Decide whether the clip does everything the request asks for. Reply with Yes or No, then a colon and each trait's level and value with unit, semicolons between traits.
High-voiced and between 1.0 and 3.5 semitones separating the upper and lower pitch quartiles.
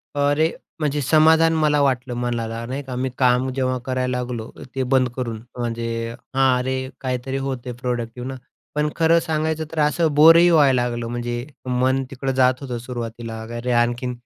No: low, 130 Hz; average, 2.8 semitones